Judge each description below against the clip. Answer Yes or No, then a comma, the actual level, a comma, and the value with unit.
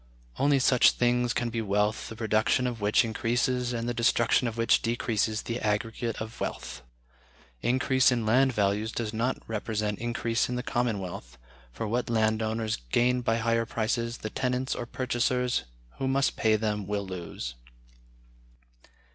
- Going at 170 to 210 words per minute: No, average, 160 wpm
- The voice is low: Yes, low, 115 Hz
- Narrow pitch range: Yes, narrow, 2.2 semitones